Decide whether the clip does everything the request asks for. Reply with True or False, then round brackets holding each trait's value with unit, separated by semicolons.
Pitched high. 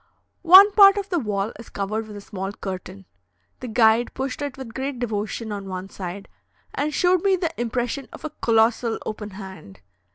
True (225 Hz)